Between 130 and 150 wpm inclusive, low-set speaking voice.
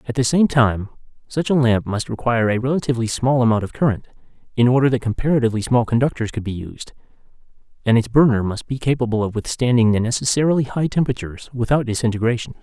No: average, 180 wpm; low, 120 Hz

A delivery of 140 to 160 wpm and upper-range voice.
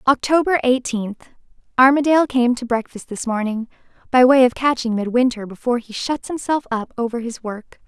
Yes: average, 150 wpm; high, 245 Hz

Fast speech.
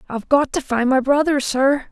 Yes: fast, 220 wpm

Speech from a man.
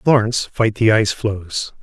Yes: male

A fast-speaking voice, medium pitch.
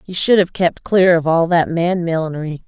Yes: fast, 225 wpm; medium, 170 Hz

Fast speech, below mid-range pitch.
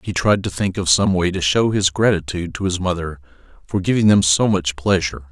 Yes: fast, 225 wpm; very low, 90 Hz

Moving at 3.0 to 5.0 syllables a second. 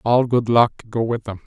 Yes: 4.7 syllables/s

